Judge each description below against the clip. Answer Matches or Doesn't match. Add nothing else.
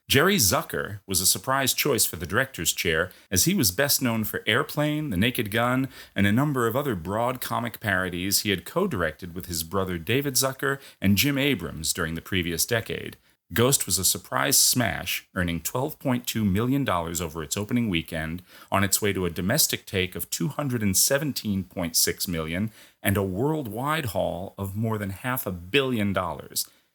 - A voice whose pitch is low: Matches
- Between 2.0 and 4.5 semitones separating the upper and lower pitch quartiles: Doesn't match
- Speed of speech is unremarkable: Matches